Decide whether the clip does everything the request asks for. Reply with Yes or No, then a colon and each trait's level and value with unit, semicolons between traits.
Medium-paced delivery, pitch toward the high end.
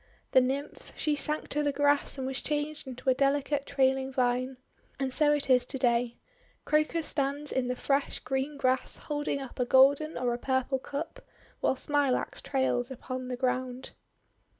Yes: average, 175 wpm; very high, 270 Hz